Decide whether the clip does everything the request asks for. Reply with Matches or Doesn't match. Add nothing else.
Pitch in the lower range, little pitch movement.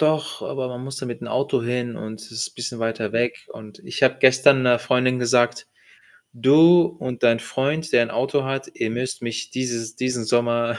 Matches